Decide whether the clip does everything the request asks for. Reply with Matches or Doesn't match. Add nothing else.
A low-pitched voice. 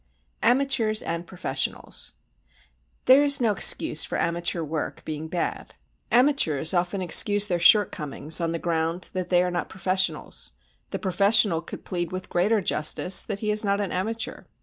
Doesn't match